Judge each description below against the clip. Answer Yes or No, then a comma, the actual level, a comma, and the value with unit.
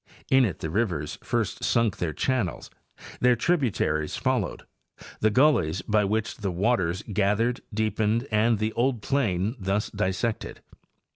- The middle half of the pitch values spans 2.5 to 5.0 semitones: Yes, average, 4.0 semitones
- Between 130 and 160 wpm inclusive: Yes, average, 140 wpm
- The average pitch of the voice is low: Yes, low, 110 Hz